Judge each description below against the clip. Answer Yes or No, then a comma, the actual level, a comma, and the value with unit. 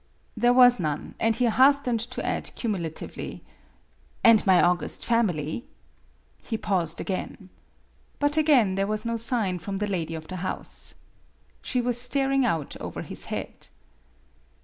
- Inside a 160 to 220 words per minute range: No, average, 150 wpm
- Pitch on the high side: Yes, high, 215 Hz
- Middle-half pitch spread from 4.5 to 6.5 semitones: Yes, wide, 5.4 semitones